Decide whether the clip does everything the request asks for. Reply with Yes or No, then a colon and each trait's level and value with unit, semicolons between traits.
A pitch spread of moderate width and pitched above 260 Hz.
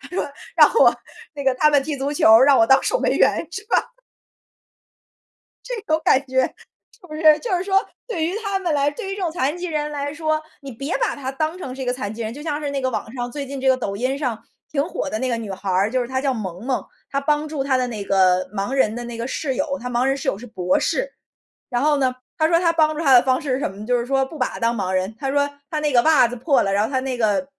Yes: average, 4.1 semitones; very high, 270 Hz